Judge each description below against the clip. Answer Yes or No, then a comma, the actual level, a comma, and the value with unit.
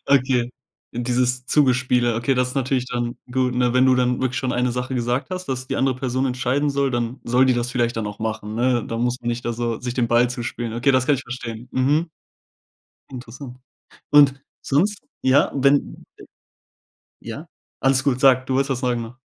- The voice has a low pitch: Yes, low, 125 Hz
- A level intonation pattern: Yes, narrow, 1.7 semitones